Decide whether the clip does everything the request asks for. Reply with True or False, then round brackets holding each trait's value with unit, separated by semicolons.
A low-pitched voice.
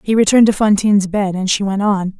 False (200 Hz)